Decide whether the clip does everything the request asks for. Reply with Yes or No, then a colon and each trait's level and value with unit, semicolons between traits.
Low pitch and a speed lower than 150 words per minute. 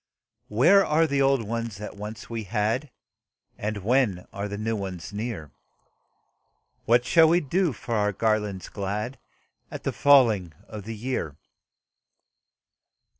Yes: low, 110 Hz; slow, 135 wpm